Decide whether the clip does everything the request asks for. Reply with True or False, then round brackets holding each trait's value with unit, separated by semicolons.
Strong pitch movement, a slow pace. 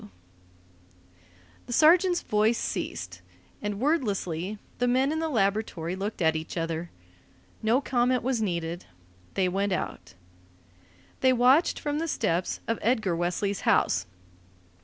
True (6.5 semitones; 130 wpm)